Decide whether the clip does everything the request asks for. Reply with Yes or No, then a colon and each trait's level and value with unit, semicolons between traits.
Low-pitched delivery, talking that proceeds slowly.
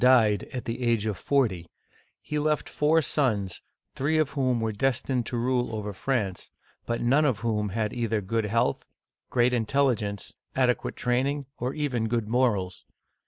No: low, 120 Hz; average, 165 wpm